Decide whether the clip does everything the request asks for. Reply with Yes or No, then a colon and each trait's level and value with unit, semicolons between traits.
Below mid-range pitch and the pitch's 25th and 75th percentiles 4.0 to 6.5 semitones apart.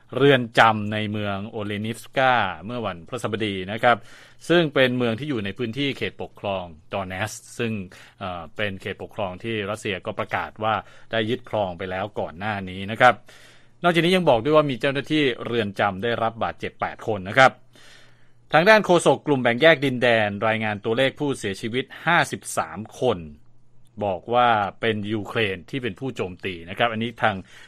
No: low, 115 Hz; average, 3.4 semitones